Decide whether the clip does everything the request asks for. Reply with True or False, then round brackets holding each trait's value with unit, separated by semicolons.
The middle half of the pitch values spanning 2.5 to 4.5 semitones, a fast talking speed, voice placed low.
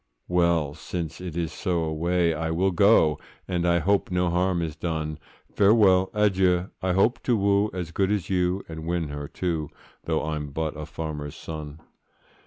False (3.0 semitones; 165 wpm; 85 Hz)